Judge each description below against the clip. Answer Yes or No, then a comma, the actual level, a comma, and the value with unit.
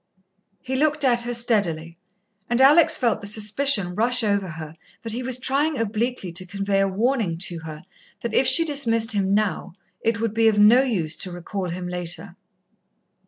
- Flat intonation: No, average, 5.2 semitones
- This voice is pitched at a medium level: No, high, 215 Hz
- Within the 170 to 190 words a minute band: Yes, average, 180 wpm